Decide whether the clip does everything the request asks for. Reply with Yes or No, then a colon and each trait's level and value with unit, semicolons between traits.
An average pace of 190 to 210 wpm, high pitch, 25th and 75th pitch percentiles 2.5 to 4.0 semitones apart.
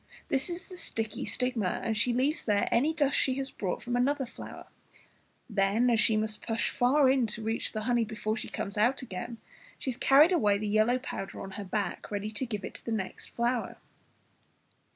Yes: average, 200 wpm; high, 230 Hz; average, 3.6 semitones